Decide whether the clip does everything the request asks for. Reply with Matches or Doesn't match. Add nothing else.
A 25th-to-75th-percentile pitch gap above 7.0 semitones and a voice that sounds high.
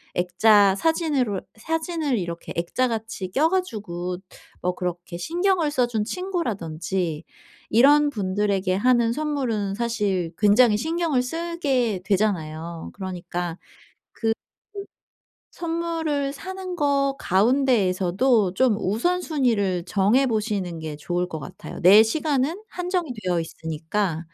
Matches